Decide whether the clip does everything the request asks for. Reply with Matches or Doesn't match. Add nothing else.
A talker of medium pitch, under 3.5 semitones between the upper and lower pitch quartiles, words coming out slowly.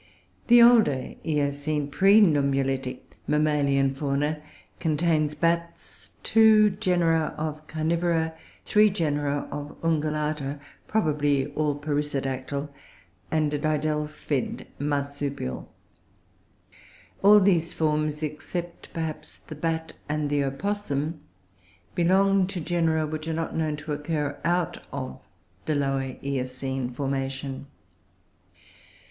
Matches